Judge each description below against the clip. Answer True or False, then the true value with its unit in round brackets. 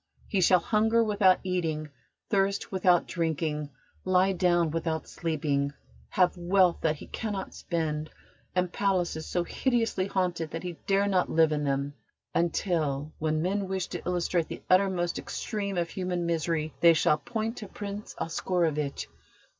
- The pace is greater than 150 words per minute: False (145 wpm)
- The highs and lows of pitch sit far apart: False (3.3 semitones)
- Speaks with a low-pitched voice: False (175 Hz)